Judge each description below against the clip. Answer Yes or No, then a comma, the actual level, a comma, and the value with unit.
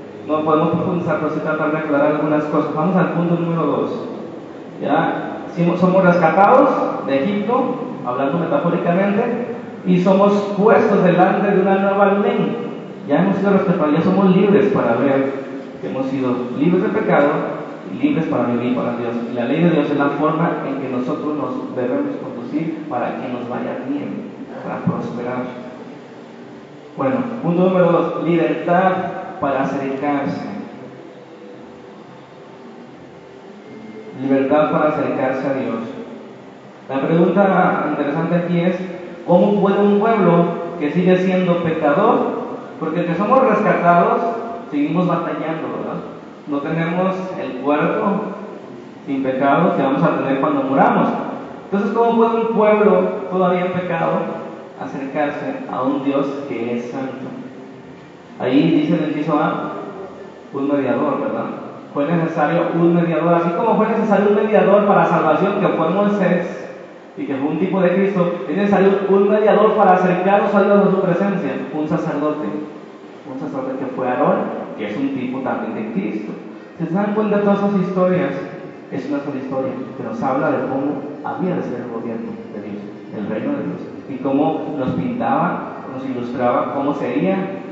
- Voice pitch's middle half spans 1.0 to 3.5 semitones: No, average, 4.8 semitones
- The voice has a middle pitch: Yes, medium, 175 Hz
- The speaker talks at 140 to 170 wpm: Yes, average, 150 wpm